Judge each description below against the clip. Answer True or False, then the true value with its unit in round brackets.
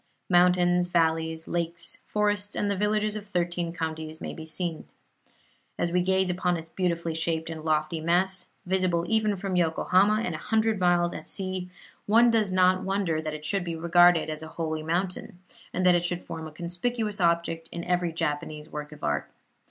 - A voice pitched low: False (175 Hz)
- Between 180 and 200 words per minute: True (185 wpm)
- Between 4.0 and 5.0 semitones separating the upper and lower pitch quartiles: False (2.6 semitones)